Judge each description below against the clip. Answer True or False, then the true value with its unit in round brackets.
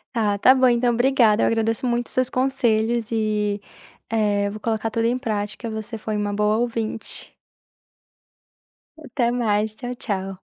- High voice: True (225 Hz)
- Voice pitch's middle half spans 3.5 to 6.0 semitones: False (2.4 semitones)